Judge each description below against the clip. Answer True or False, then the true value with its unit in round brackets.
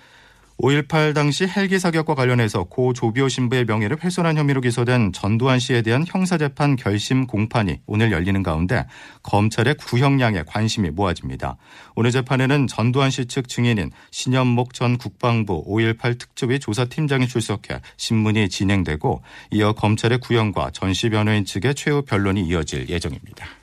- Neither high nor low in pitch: False (120 Hz)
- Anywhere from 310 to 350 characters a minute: True (345 characters per minute)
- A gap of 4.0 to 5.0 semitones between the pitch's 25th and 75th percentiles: True (4.3 semitones)